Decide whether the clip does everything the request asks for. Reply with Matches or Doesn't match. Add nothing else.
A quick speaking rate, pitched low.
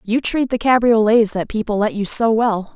Doesn't match